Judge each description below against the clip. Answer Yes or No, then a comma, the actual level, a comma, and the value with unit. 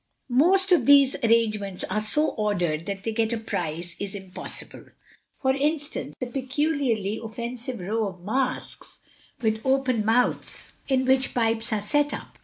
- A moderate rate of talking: Yes, average, 150 wpm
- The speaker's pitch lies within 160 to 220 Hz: No, high, 230 Hz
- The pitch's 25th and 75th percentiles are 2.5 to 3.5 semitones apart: No, average, 4.2 semitones